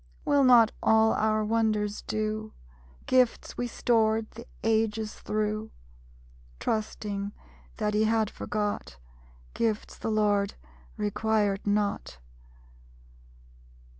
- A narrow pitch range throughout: Yes, narrow, 1.0 semitones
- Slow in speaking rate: Yes, slow, 95 wpm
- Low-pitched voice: No, high, 215 Hz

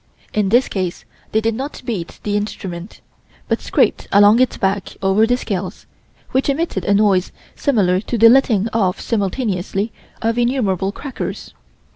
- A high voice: Yes, high, 210 Hz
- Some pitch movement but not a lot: Yes, average, 3.7 semitones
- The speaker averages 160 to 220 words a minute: No, average, 150 wpm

